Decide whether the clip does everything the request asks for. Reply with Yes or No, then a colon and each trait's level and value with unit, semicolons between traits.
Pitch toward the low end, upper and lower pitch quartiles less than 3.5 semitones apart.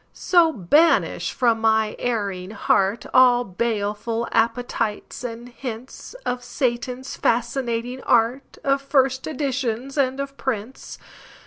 No: high, 245 Hz; average, 2.9 semitones